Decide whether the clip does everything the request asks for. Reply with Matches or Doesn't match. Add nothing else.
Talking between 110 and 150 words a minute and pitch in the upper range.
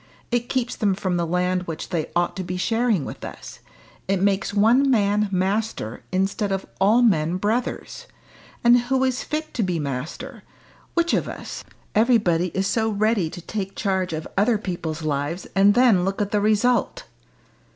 Doesn't match